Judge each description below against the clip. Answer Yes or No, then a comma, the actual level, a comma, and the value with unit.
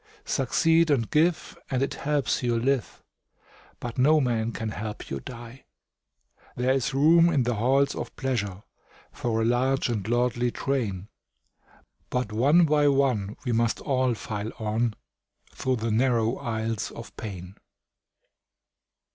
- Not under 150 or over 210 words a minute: No, average, 140 wpm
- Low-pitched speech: Yes, low, 120 Hz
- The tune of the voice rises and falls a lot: No, average, 3.3 semitones